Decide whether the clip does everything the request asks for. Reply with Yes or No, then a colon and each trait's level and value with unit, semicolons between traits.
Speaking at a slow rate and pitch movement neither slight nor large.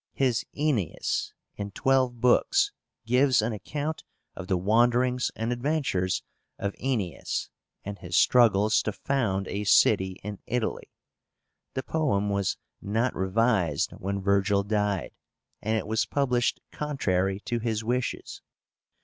Yes: slow, 125 wpm; average, 4.1 semitones